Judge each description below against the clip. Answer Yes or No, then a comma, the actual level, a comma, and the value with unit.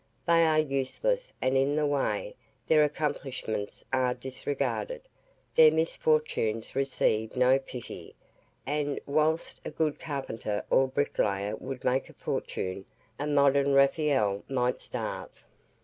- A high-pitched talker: No, medium, 140 Hz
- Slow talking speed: Yes, slow, 120 wpm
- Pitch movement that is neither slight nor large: Yes, average, 3.3 semitones